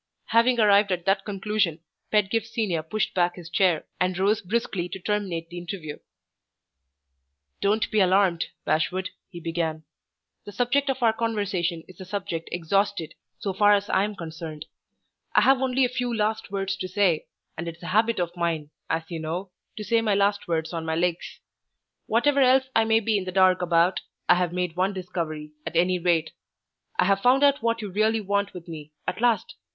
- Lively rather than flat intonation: No, average, 3.8 semitones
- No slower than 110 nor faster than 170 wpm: No, average, 190 wpm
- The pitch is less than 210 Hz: Yes, high, 190 Hz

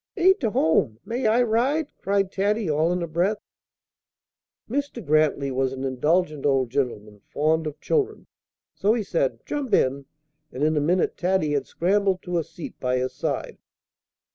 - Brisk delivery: No, average, 165 wpm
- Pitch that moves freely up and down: Yes, wide, 7.0 semitones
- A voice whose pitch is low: No, medium, 170 Hz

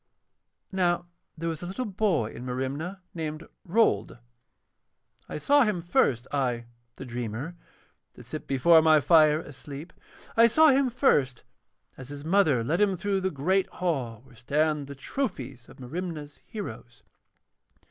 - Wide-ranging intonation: Yes, wide, 6.0 semitones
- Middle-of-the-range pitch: Yes, medium, 155 Hz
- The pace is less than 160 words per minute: Yes, average, 145 wpm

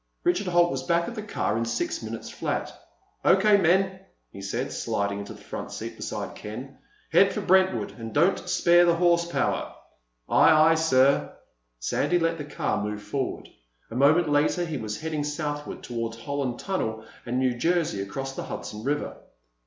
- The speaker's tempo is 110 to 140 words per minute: No, average, 175 wpm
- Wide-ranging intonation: Yes, wide, 6.9 semitones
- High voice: No, medium, 145 Hz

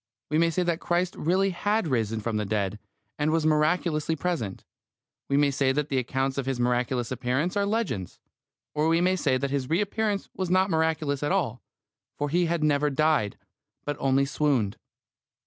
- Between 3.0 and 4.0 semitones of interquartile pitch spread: No, average, 4.8 semitones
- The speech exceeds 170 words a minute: Yes, average, 180 wpm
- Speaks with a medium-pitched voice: Yes, medium, 150 Hz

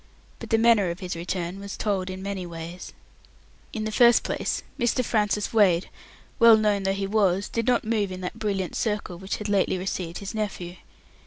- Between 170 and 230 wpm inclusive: Yes, average, 190 wpm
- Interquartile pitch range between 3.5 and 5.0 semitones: No, average, 2.9 semitones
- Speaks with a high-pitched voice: Yes, high, 200 Hz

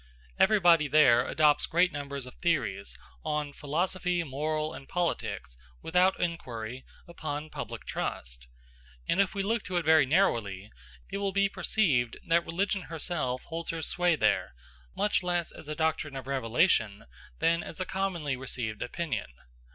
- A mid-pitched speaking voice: Yes, medium, 155 Hz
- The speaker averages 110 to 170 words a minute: Yes, average, 150 wpm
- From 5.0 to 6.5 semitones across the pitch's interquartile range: Yes, average, 5.3 semitones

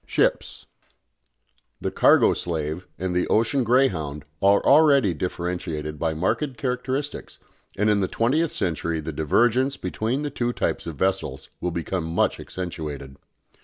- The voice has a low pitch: Yes, very low, 95 Hz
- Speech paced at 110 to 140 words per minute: Yes, slow, 135 wpm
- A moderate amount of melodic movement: No, wide, 7.3 semitones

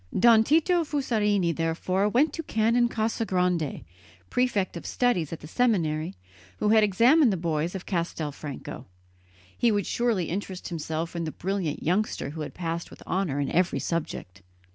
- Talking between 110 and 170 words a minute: Yes, average, 155 wpm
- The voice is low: No, medium, 185 Hz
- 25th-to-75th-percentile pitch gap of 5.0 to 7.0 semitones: Yes, wide, 5.4 semitones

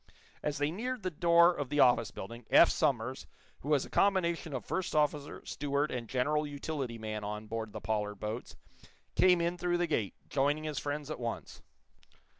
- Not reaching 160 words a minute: No, average, 185 wpm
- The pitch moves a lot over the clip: Yes, wide, 6.1 semitones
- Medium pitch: Yes, medium, 145 Hz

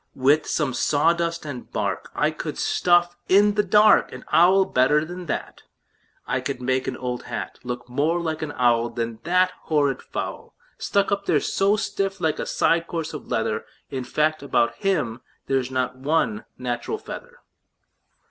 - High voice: No, medium, 155 Hz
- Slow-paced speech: No, average, 165 wpm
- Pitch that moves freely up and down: Yes, wide, 5.9 semitones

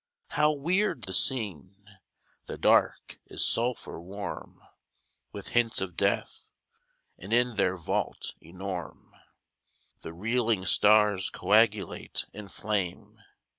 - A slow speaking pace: Yes, slow, 105 wpm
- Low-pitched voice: Yes, low, 105 Hz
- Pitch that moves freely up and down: No, average, 4.0 semitones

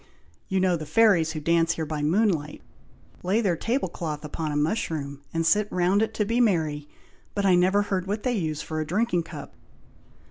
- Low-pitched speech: No, medium, 175 Hz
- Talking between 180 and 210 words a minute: Yes, average, 200 wpm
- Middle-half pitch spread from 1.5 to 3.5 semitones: No, average, 4.6 semitones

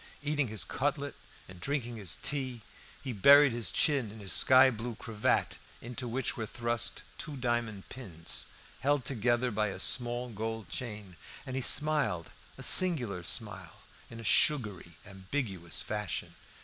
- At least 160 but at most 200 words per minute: No, average, 150 wpm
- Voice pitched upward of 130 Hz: No, low, 120 Hz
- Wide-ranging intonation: No, average, 4.3 semitones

